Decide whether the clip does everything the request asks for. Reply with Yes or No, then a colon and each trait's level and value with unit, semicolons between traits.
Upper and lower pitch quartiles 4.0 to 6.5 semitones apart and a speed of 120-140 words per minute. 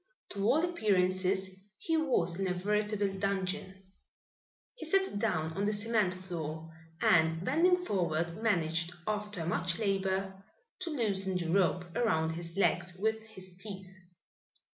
No: average, 3.2 semitones; slow, 135 wpm